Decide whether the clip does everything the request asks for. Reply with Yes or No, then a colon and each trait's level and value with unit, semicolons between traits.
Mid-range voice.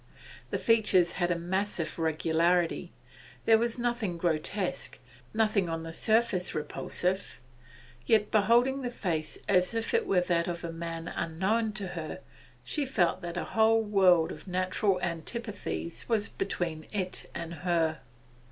Yes: medium, 180 Hz